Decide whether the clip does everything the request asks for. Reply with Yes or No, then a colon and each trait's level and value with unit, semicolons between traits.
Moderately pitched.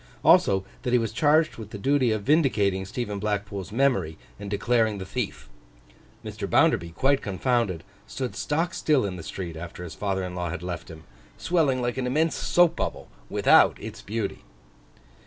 No: low, 105 Hz